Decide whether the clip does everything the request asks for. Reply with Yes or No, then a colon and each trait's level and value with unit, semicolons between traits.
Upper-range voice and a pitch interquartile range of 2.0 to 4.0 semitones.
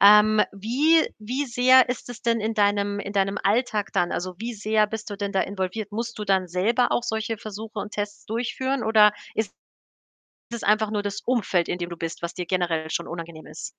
Yes: high, 210 Hz; narrow, 2.6 semitones